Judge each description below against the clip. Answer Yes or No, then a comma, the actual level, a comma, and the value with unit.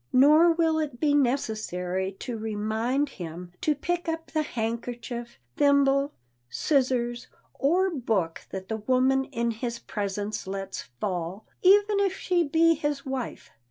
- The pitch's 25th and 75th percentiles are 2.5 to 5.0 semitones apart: No, wide, 5.6 semitones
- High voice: Yes, very high, 255 Hz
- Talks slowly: Yes, slow, 130 wpm